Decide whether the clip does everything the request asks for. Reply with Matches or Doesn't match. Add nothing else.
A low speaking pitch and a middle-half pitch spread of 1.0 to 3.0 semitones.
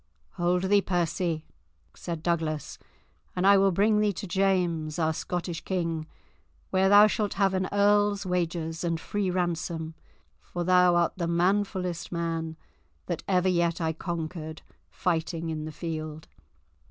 Doesn't match